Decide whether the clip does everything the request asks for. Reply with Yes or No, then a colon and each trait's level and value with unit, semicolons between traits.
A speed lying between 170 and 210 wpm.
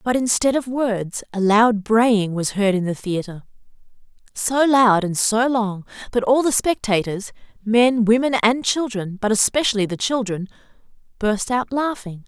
No: average, 145 wpm